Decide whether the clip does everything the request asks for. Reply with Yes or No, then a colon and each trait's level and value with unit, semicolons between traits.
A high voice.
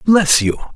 No: medium, 160 Hz